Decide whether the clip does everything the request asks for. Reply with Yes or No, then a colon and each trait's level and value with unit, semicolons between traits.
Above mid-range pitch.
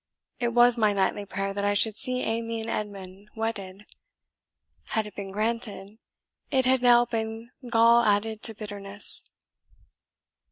Yes: high, 220 Hz